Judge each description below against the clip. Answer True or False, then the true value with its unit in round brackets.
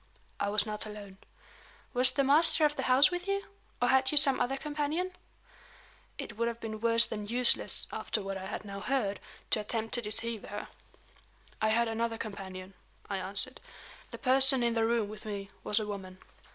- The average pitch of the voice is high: True (230 Hz)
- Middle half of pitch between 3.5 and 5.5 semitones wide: True (4.2 semitones)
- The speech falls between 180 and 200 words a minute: True (190 wpm)